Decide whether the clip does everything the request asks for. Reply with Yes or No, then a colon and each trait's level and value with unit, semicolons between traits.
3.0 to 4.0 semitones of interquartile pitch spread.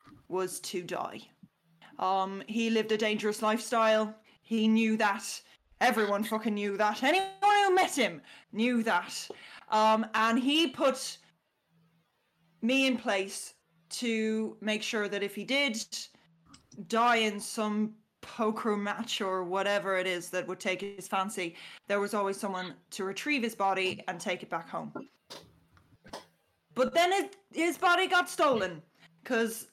Yes: average, 3.3 semitones